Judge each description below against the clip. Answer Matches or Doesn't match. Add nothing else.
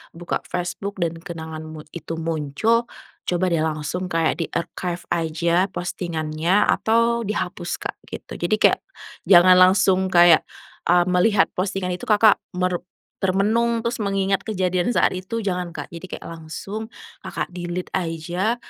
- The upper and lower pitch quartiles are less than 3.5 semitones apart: Matches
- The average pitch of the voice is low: Doesn't match